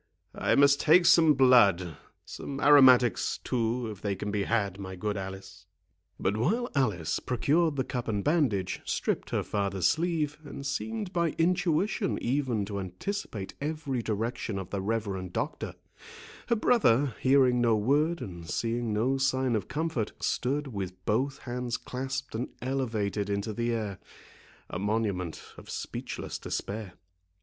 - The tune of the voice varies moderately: No, wide, 5.8 semitones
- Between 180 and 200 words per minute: No, average, 145 wpm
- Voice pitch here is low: Yes, low, 120 Hz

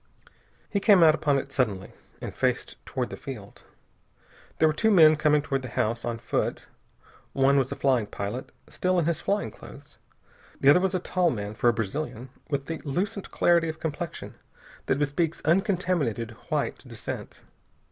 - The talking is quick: No, average, 170 wpm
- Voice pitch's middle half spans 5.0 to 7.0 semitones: Yes, average, 5.3 semitones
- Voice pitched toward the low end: No, medium, 145 Hz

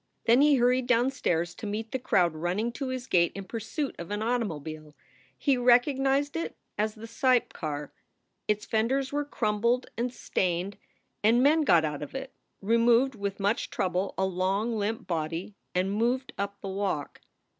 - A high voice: Yes, high, 220 Hz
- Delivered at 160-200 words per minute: Yes, average, 165 wpm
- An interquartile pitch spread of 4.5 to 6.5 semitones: Yes, average, 5.1 semitones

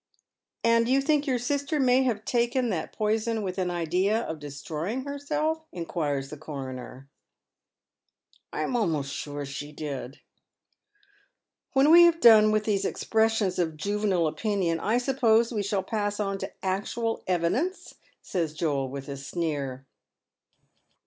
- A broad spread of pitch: Yes, wide, 7.6 semitones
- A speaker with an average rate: Yes, average, 155 wpm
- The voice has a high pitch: Yes, high, 205 Hz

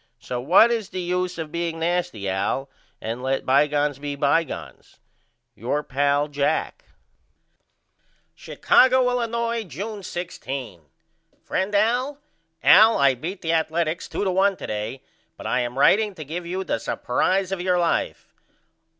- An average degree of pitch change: No, wide, 5.7 semitones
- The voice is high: No, medium, 170 Hz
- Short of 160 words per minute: Yes, average, 150 wpm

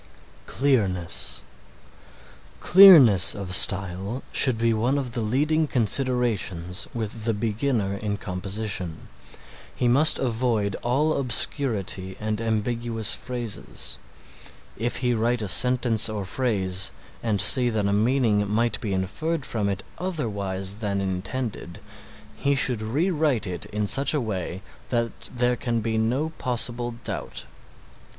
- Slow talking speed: Yes, slow, 130 wpm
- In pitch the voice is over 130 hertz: No, low, 110 Hz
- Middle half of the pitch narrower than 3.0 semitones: No, average, 3.8 semitones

